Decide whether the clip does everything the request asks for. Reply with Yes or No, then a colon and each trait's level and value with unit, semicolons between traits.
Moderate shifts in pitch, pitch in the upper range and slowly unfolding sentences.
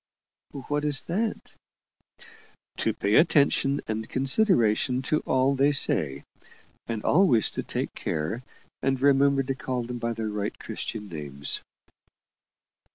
No: average, 4.5 semitones; low, 130 Hz; slow, 125 wpm